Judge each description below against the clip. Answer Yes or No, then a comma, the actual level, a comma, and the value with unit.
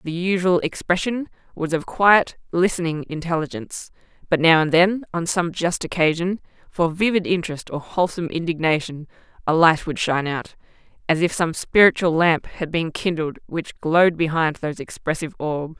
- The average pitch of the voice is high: No, medium, 170 Hz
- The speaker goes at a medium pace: Yes, average, 155 wpm